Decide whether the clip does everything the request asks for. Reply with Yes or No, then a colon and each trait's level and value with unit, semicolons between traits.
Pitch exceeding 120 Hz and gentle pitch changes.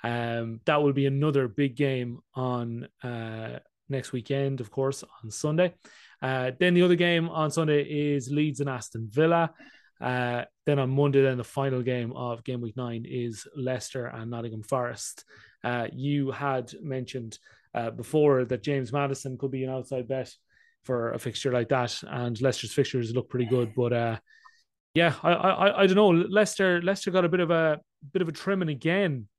No: low, 135 Hz; average, 3.9 semitones